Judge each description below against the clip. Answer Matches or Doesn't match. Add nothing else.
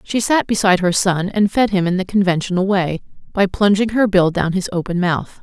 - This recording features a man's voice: Doesn't match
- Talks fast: Matches